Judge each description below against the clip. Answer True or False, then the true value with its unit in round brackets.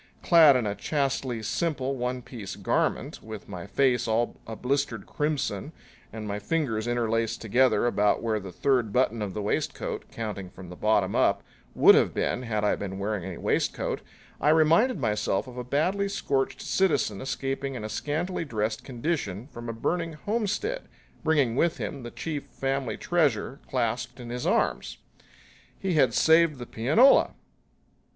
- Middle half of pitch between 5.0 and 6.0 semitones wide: True (5.3 semitones)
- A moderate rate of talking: True (160 wpm)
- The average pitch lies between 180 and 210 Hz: False (125 Hz)